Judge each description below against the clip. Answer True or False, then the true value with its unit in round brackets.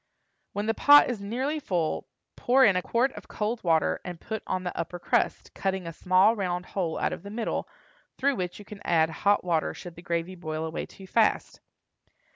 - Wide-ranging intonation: False (4.2 semitones)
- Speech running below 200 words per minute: False (205 wpm)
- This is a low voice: False (185 Hz)